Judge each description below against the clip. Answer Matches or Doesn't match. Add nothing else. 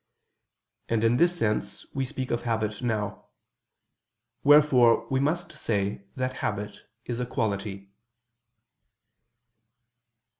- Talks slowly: Matches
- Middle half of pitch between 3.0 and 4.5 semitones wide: Matches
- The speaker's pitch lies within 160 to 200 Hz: Doesn't match